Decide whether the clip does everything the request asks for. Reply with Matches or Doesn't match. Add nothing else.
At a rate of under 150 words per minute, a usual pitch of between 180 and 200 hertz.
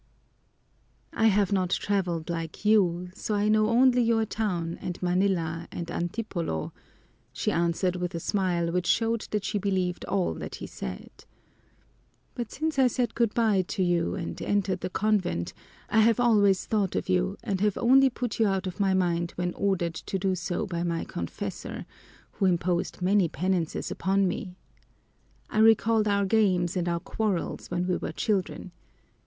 Doesn't match